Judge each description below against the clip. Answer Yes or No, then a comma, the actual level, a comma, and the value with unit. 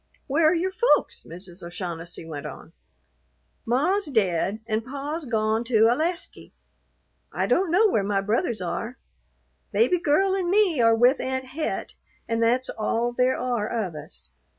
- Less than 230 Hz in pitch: No, high, 240 Hz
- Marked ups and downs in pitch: Yes, wide, 7.0 semitones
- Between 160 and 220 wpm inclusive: No, average, 150 wpm